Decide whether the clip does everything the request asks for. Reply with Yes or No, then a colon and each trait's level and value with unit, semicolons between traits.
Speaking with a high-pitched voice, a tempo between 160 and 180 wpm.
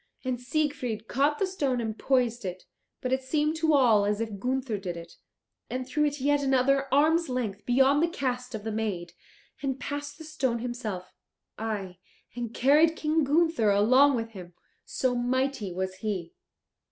Yes: very high, 255 Hz; average, 170 wpm